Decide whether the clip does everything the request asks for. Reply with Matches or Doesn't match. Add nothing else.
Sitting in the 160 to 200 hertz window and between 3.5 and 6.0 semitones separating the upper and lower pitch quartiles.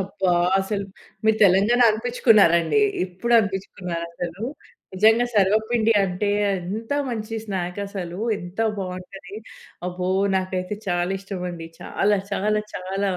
Doesn't match